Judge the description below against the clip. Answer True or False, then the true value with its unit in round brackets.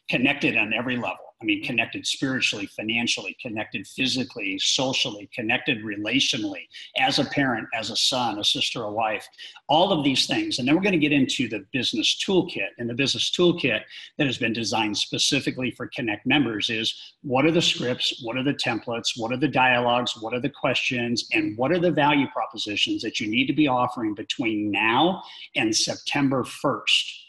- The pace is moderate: True (185 wpm)